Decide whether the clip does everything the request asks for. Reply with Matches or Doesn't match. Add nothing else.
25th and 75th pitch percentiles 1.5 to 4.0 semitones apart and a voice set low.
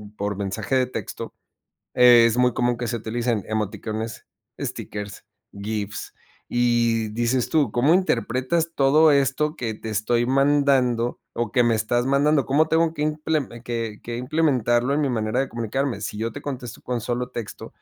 Matches